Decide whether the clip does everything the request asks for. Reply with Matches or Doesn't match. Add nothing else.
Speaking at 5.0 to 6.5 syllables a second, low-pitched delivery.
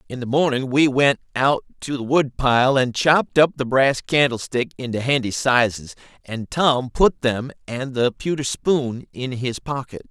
Doesn't match